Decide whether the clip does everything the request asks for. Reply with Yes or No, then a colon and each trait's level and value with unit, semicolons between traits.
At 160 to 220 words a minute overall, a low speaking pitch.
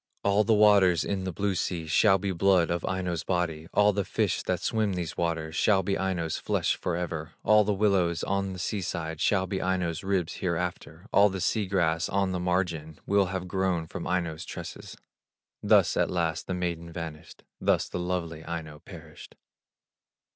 Yes: average, 180 wpm; very low, 90 Hz